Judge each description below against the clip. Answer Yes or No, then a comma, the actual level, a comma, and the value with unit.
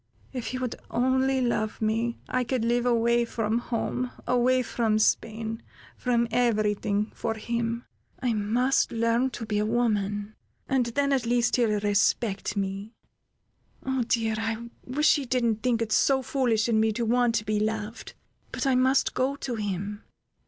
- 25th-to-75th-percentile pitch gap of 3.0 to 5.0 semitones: No, narrow, 2.4 semitones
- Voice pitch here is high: Yes, high, 235 Hz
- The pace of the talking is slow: No, average, 165 wpm